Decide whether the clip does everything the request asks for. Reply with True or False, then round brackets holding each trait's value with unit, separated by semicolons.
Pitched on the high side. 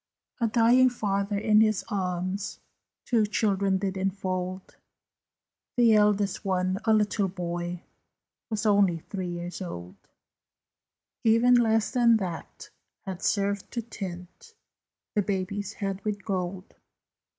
True (200 Hz)